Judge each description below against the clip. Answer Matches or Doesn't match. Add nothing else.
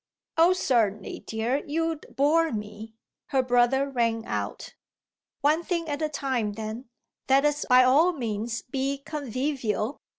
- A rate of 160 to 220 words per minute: Doesn't match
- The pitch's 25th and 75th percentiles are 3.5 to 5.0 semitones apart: Matches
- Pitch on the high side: Matches